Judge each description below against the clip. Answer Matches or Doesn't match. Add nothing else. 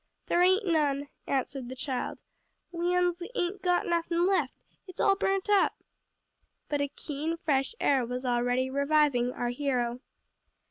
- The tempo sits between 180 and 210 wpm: Doesn't match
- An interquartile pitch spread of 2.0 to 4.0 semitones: Doesn't match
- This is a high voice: Matches